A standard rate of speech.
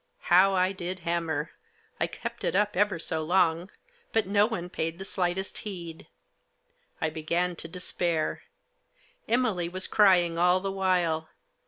Yes: average, 145 wpm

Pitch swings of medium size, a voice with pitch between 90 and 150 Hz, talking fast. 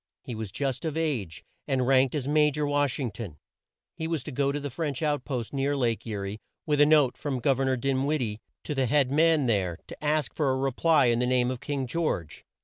Yes: average, 3.3 semitones; low, 135 Hz; fast, 255 wpm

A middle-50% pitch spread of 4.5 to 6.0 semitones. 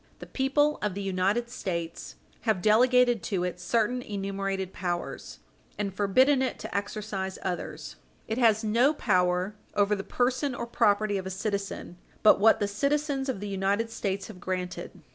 No: average, 4.0 semitones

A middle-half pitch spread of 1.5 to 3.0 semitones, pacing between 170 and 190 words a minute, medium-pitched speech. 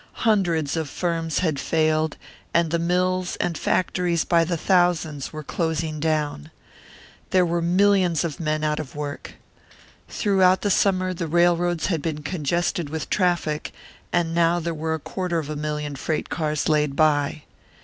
No: narrow, 2.5 semitones; average, 160 wpm; medium, 165 Hz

